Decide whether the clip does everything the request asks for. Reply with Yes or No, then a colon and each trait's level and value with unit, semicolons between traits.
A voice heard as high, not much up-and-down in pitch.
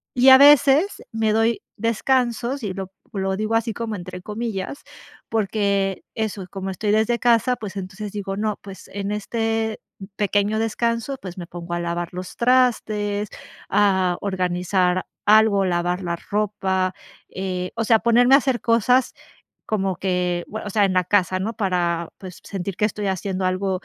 No: high, 205 Hz; average, 3.2 semitones